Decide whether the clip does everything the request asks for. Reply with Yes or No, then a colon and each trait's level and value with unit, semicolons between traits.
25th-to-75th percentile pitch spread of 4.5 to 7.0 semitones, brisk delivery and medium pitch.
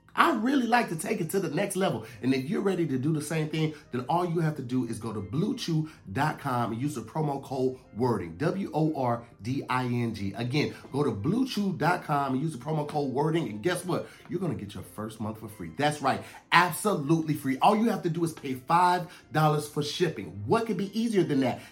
Yes: wide, 5.5 semitones; fast, 230 wpm; medium, 150 Hz